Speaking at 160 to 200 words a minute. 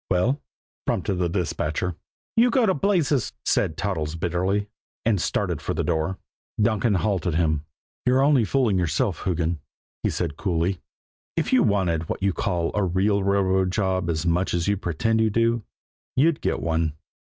Yes: average, 165 wpm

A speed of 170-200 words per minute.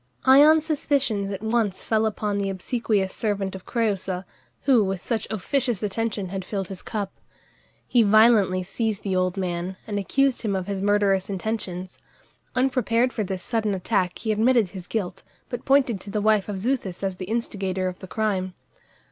Yes: average, 175 wpm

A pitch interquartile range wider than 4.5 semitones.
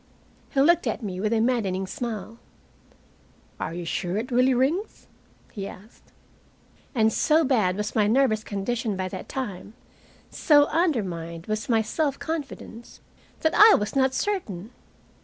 Yes: wide, 5.4 semitones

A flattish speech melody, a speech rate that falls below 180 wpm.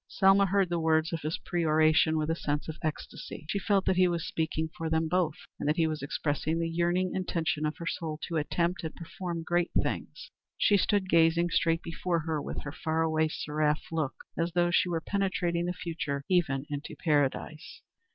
No: narrow, 1.9 semitones; average, 200 wpm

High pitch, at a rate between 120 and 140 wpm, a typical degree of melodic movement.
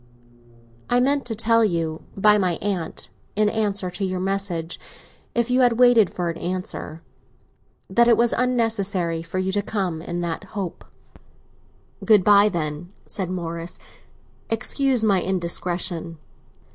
Yes: high, 195 Hz; slow, 135 wpm; average, 4.4 semitones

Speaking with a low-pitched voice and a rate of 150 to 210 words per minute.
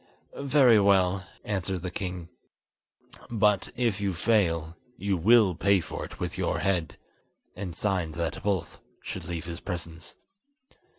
No: very low, 95 Hz; slow, 135 wpm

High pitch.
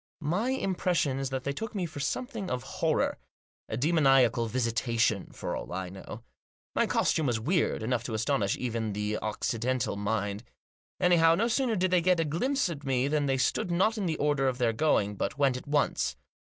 No: low, 135 Hz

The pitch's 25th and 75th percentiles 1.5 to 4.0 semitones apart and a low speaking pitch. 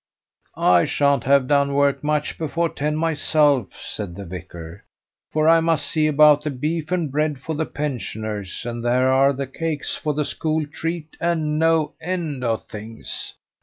No: average, 3.5 semitones; medium, 145 Hz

